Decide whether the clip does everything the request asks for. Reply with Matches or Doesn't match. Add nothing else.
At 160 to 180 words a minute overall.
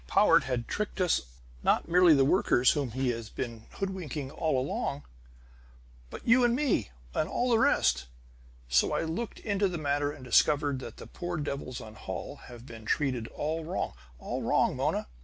Matches